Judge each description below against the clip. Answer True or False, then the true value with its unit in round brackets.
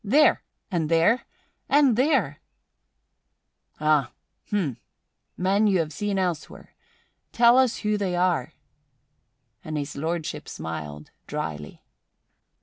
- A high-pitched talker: False (175 Hz)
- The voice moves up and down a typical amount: False (6.1 semitones)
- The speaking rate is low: True (105 wpm)